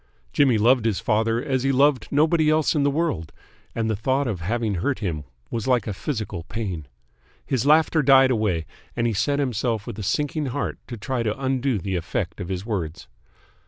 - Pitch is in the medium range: No, low, 120 Hz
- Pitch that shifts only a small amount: No, average, 5.1 semitones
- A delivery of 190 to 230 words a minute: Yes, average, 195 wpm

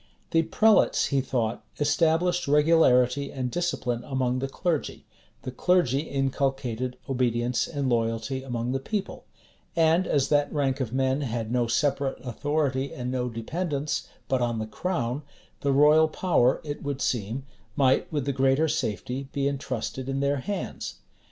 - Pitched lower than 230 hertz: Yes, low, 135 Hz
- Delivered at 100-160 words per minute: Yes, average, 150 wpm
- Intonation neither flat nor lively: Yes, average, 3.0 semitones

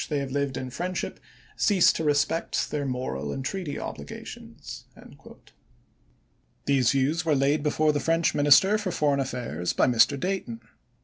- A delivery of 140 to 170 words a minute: Yes, average, 165 wpm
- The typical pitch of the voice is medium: Yes, medium, 145 Hz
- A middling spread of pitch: Yes, average, 3.7 semitones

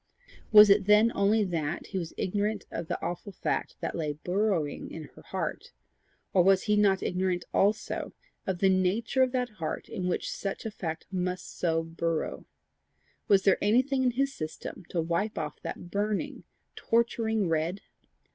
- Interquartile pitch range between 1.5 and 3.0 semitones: No, average, 3.7 semitones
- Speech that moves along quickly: No, average, 165 wpm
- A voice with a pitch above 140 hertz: Yes, high, 190 Hz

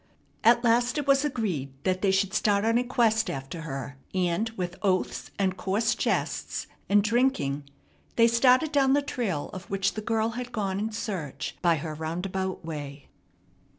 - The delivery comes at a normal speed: Yes, average, 170 wpm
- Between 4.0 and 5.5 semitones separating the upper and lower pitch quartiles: Yes, average, 5.2 semitones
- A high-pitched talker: Yes, high, 200 Hz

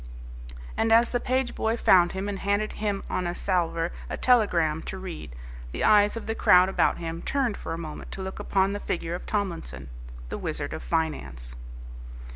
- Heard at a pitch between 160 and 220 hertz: Yes, high, 190 Hz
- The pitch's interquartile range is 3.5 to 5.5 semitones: Yes, average, 4.1 semitones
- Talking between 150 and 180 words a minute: No, average, 190 wpm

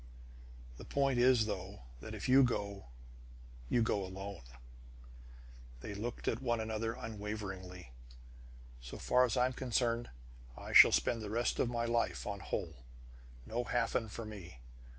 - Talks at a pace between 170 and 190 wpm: No, average, 145 wpm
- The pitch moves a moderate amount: Yes, average, 3.2 semitones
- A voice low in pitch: Yes, low, 110 Hz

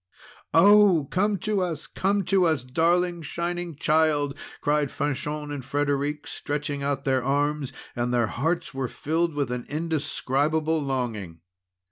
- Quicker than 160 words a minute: No, slow, 135 wpm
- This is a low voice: No, medium, 150 Hz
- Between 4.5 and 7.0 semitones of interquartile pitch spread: No, average, 3.5 semitones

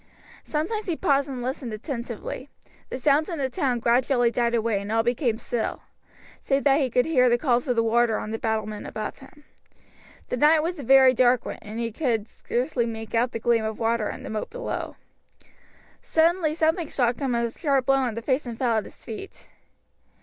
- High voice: Yes, high, 245 Hz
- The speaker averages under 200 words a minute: No, fast, 205 wpm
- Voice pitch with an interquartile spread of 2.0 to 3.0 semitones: No, average, 3.4 semitones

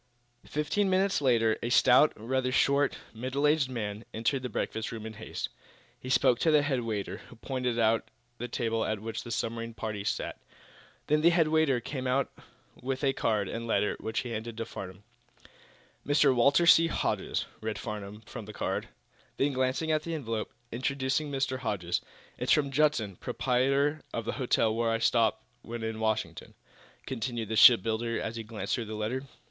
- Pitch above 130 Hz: No, low, 120 Hz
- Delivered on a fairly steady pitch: No, average, 3.7 semitones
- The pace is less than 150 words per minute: No, average, 180 wpm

